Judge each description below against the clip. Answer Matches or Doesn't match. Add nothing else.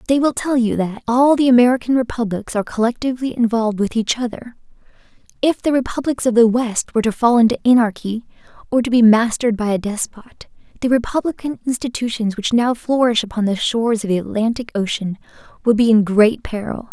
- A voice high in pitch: Matches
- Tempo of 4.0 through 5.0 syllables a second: Doesn't match